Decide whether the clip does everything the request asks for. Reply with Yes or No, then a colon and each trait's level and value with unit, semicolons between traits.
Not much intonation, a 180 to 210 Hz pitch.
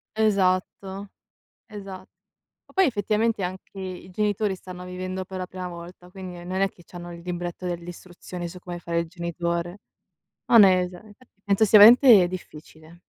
Yes: narrow, 2.2 semitones; medium, 185 Hz